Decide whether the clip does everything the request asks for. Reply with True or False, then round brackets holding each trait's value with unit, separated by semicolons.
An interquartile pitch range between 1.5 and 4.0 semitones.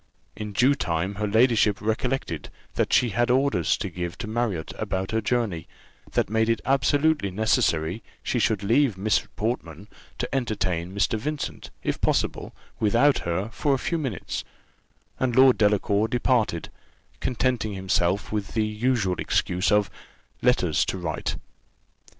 False (4.5 semitones)